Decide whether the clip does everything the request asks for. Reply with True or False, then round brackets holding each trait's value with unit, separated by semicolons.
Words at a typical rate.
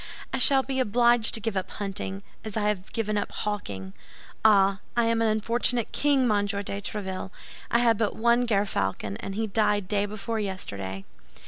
True (180 wpm)